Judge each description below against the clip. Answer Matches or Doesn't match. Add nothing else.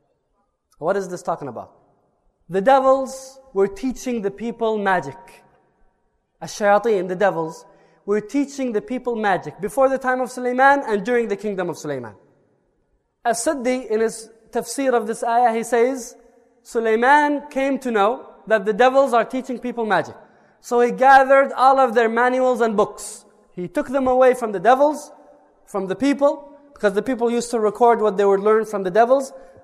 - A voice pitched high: Matches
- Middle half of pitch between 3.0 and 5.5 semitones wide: Matches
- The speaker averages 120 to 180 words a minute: Matches